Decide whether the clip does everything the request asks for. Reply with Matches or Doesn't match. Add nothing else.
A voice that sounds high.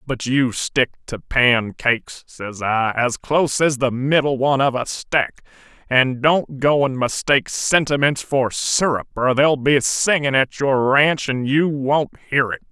Doesn't match